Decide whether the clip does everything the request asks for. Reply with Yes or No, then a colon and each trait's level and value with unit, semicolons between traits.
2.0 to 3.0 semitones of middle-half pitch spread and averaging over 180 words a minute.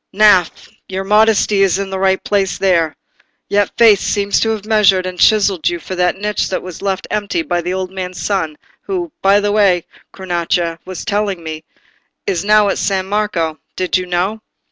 Yes: narrow, 2.4 semitones; average, 190 wpm